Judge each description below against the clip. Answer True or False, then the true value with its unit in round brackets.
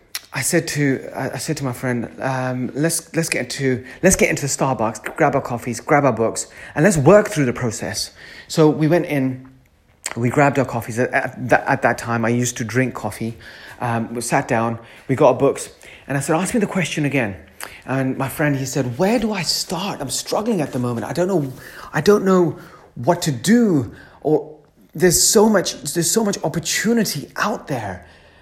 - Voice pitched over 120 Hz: True (140 Hz)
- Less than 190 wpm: False (200 wpm)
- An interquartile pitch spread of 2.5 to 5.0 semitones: False (5.4 semitones)